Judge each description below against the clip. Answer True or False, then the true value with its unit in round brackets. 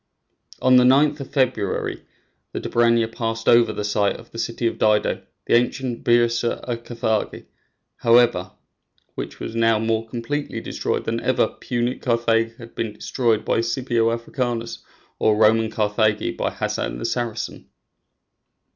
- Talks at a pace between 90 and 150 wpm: True (145 wpm)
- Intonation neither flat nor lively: False (1.3 semitones)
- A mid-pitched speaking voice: False (115 Hz)